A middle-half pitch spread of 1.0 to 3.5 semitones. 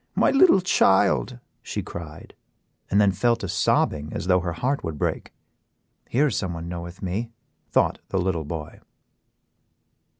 No: average, 5.2 semitones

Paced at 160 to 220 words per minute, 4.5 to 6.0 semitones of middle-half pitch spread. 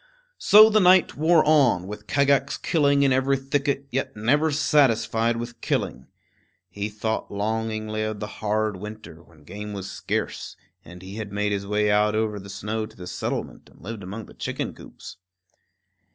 Yes: average, 170 wpm; average, 4.8 semitones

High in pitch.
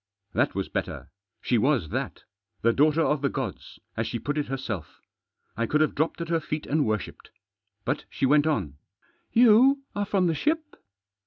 No: medium, 150 Hz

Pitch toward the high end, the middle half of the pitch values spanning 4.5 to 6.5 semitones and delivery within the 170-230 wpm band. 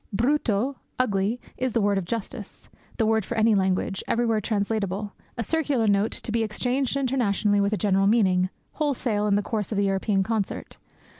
No: high, 215 Hz; average, 2.9 semitones; average, 175 wpm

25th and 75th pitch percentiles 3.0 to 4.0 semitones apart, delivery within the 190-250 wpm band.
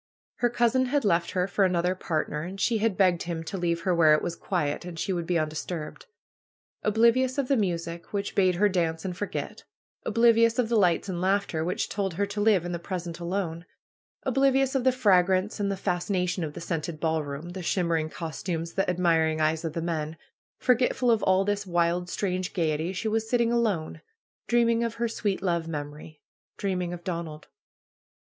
Yes: average, 3.7 semitones; average, 200 wpm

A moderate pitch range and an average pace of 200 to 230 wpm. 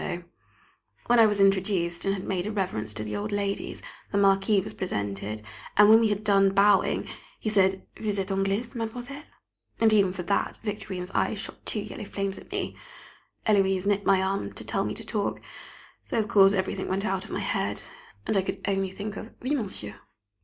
No: narrow, 1.8 semitones; fast, 205 wpm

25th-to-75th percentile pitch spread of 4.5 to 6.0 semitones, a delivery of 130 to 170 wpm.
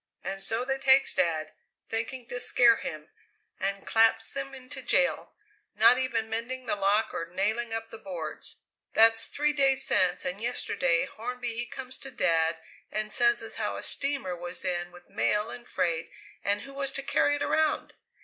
No: average, 5.1 semitones; average, 180 wpm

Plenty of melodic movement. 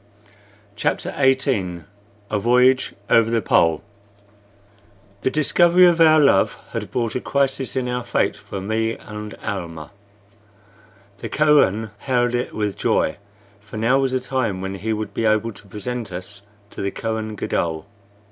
No: average, 4.4 semitones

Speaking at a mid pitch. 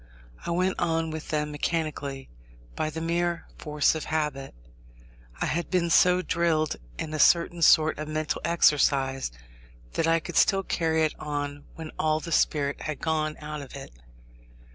Yes: medium, 155 Hz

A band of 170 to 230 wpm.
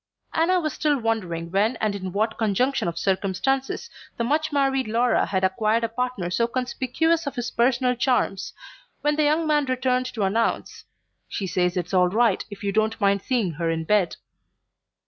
Yes: average, 180 wpm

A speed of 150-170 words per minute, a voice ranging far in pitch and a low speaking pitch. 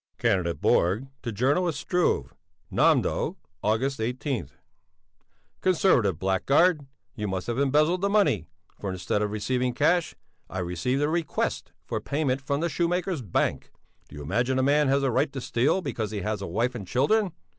Yes: average, 165 wpm; wide, 6.4 semitones; low, 130 Hz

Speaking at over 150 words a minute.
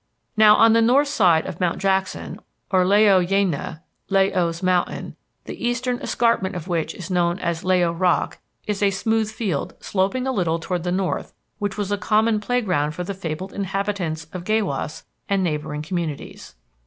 Yes: average, 180 wpm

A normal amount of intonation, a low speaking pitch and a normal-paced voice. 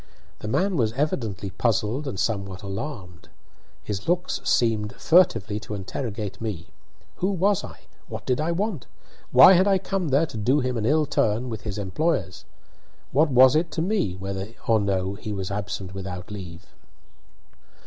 No: wide, 7.5 semitones; low, 110 Hz; average, 165 wpm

